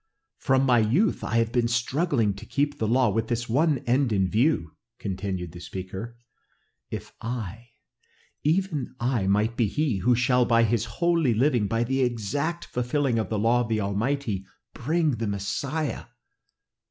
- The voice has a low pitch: Yes, low, 120 Hz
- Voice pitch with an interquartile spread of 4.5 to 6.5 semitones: No, average, 4.1 semitones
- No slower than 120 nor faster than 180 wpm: Yes, average, 165 wpm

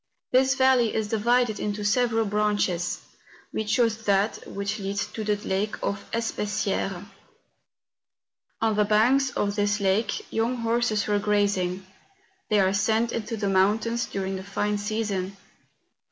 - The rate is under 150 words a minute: Yes, average, 140 wpm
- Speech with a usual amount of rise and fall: No, narrow, 2.2 semitones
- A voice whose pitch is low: No, high, 210 Hz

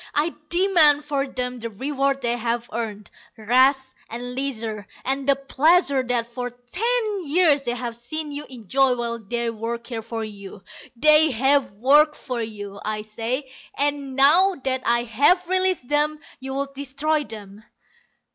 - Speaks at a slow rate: No, average, 155 wpm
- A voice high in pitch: Yes, very high, 260 Hz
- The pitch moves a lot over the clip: No, average, 3.9 semitones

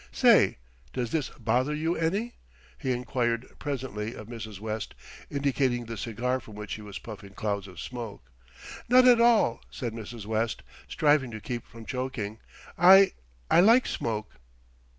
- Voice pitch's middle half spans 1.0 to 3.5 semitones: No, average, 4.7 semitones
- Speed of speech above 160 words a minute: No, average, 150 wpm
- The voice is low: Yes, low, 120 Hz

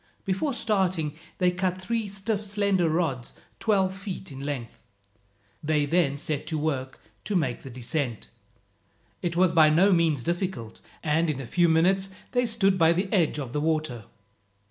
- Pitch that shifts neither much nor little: Yes, average, 4.5 semitones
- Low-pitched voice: No, medium, 170 Hz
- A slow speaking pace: No, average, 165 wpm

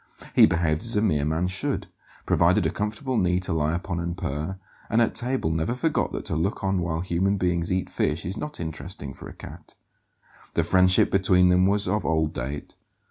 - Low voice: Yes, very low, 90 Hz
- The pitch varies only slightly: No, average, 3.4 semitones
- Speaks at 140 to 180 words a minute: No, average, 200 wpm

